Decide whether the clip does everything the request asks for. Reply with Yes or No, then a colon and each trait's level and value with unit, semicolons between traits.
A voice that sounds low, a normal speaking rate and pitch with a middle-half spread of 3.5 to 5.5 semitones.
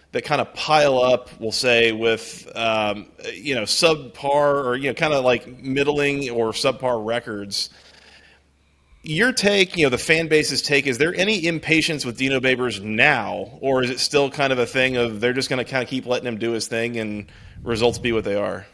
No: low, 125 Hz; fast, 210 wpm; average, 3.8 semitones